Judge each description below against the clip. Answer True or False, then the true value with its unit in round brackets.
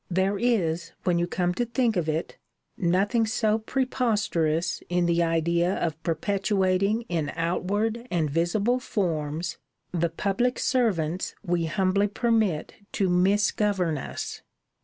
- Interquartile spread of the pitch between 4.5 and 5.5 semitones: False (4.1 semitones)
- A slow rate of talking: True (125 wpm)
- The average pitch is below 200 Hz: True (185 Hz)